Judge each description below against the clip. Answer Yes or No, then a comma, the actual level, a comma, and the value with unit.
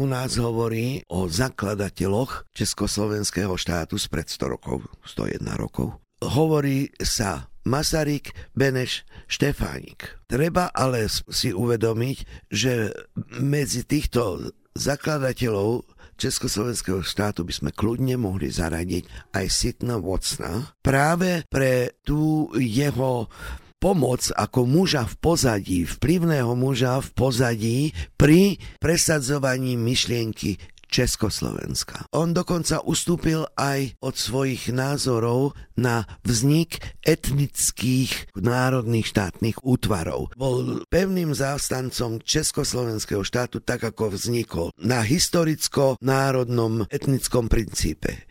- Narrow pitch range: No, average, 4.8 semitones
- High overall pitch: No, low, 125 Hz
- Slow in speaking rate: Yes, slow, 95 wpm